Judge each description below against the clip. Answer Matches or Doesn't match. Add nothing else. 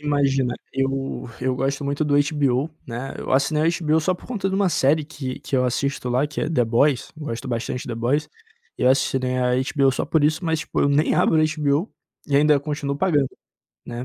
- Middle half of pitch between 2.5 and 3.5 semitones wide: Matches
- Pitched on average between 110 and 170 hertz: Matches